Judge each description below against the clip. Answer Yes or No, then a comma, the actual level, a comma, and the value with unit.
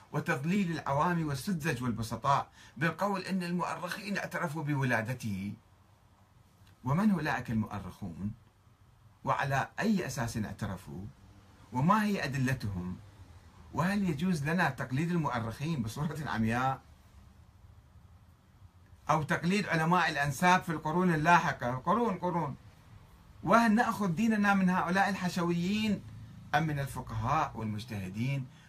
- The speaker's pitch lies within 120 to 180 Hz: Yes, medium, 140 Hz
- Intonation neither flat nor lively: No, wide, 8.5 semitones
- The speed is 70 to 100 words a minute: Yes, average, 95 wpm